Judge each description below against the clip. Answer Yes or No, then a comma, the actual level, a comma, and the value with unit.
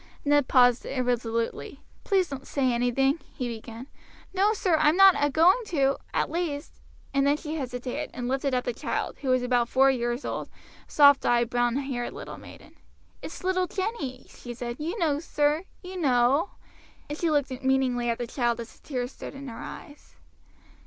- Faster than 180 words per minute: Yes, average, 190 wpm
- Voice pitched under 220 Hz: No, very high, 270 Hz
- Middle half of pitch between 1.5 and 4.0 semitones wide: Yes, average, 3.6 semitones